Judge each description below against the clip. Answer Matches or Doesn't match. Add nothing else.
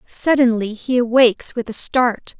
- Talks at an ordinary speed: Matches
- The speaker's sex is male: Doesn't match